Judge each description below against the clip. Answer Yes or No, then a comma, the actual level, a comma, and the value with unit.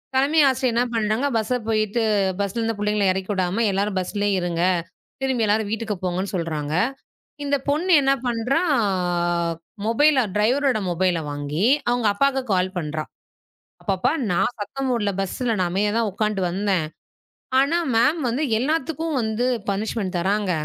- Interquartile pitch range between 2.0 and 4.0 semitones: No, average, 4.8 semitones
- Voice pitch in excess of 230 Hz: No, high, 215 Hz